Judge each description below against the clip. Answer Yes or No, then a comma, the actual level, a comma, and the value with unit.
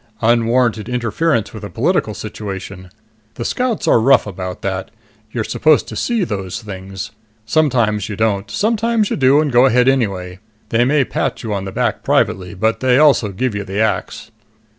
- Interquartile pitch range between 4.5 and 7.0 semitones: Yes, average, 5.0 semitones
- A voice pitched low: Yes, low, 115 Hz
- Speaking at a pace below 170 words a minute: No, average, 175 wpm